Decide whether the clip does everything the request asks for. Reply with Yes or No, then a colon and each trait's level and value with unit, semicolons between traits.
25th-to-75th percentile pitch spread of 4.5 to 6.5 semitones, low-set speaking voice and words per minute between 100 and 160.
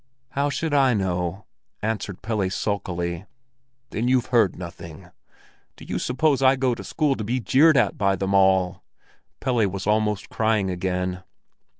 Yes: average, 5.2 semitones; low, 105 Hz; average, 155 wpm